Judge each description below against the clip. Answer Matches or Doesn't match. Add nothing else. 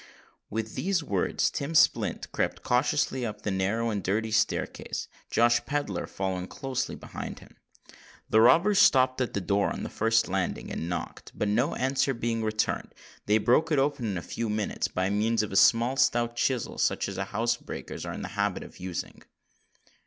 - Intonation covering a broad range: Doesn't match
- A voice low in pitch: Matches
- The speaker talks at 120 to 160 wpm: Doesn't match